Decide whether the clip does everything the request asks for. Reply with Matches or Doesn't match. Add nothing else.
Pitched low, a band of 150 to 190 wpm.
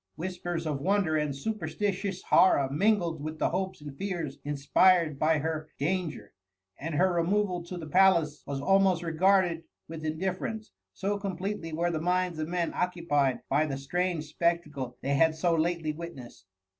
Doesn't match